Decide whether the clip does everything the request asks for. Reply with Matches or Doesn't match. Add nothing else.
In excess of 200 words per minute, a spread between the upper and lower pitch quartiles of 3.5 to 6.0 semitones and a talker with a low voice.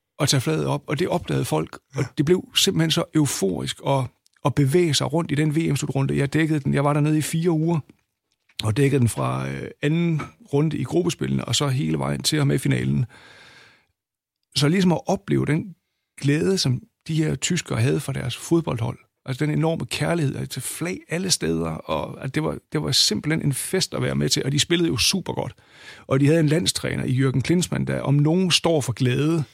Doesn't match